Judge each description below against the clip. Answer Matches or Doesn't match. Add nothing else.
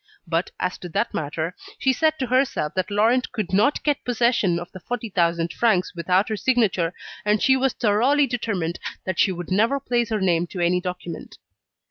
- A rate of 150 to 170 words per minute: Doesn't match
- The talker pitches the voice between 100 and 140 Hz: Doesn't match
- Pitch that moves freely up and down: Matches